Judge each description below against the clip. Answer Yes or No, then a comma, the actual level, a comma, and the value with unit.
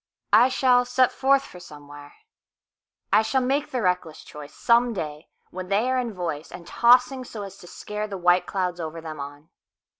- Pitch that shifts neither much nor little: No, wide, 7.2 semitones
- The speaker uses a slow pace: No, average, 160 wpm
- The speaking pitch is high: Yes, high, 195 Hz